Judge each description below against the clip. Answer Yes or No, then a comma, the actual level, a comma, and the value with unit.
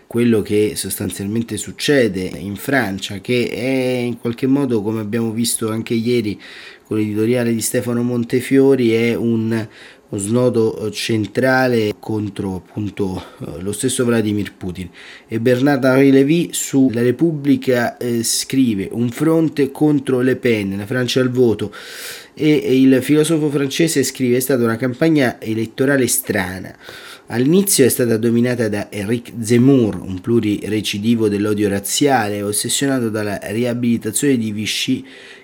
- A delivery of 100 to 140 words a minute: Yes, average, 130 wpm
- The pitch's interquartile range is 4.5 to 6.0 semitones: No, average, 3.7 semitones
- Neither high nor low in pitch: No, low, 120 Hz